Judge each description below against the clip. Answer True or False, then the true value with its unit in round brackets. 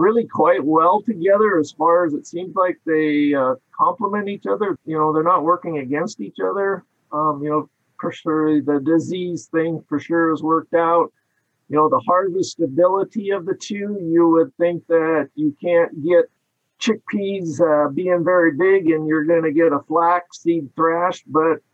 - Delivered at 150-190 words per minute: True (180 wpm)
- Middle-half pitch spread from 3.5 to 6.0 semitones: False (2.9 semitones)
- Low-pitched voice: False (165 Hz)